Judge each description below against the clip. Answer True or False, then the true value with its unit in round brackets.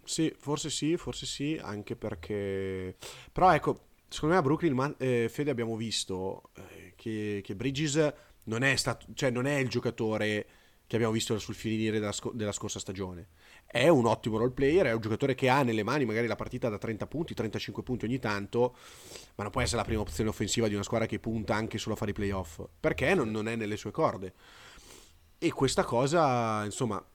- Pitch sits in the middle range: False (115 Hz)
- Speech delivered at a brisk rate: True (200 wpm)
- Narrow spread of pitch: False (3.8 semitones)